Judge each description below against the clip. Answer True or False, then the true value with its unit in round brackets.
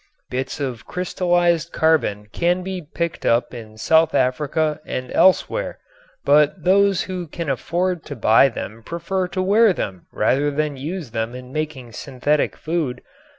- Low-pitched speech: False (155 Hz)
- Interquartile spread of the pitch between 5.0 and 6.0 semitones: True (5.6 semitones)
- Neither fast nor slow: True (150 wpm)